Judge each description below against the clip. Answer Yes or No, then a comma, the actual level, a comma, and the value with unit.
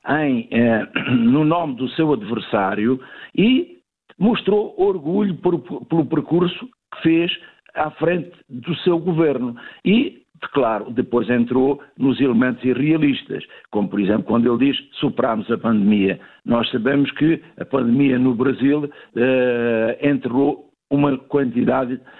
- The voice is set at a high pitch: No, low, 135 Hz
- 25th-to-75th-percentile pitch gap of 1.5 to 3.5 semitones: No, average, 4.8 semitones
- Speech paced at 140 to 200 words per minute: No, average, 130 wpm